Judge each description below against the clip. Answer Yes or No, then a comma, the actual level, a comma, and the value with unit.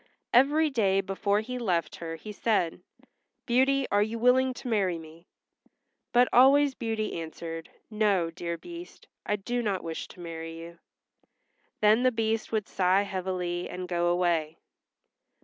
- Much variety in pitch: Yes, wide, 5.7 semitones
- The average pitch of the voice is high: Yes, high, 200 Hz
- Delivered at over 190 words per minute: No, average, 150 wpm